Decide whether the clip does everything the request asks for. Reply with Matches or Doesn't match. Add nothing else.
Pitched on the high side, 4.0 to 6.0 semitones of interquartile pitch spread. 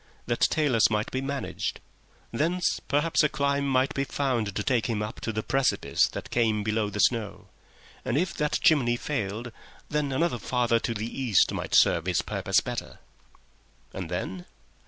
Doesn't match